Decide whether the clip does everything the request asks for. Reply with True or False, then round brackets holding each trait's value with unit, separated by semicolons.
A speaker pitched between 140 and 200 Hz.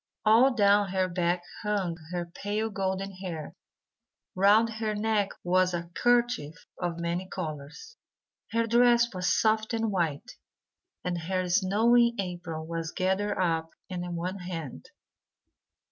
True (185 Hz)